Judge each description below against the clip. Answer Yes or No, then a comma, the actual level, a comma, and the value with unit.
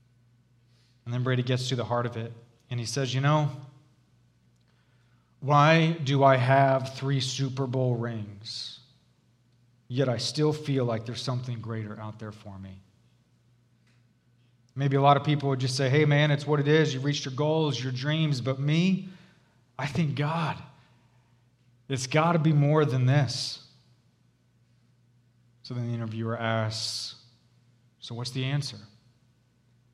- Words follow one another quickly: No, average, 150 wpm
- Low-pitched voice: Yes, low, 125 Hz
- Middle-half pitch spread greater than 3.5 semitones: No, narrow, 2.5 semitones